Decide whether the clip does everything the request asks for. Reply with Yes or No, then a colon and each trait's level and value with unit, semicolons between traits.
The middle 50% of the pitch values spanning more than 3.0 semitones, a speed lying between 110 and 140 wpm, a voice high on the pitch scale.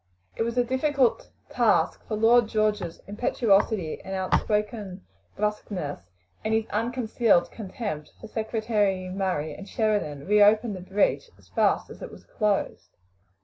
No: average, 2.7 semitones; slow, 135 wpm; high, 210 Hz